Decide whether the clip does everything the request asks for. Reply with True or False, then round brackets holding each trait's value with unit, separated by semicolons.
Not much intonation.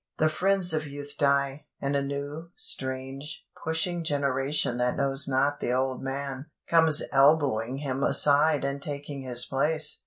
True (2.1 semitones)